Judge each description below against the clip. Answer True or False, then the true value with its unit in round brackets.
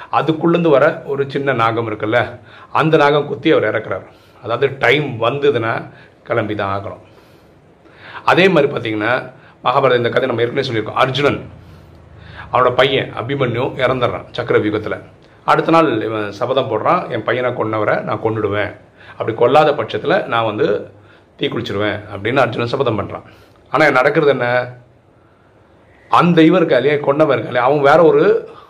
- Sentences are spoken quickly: True (135 wpm)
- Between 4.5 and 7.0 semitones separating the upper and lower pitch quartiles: True (4.8 semitones)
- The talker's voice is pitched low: True (125 Hz)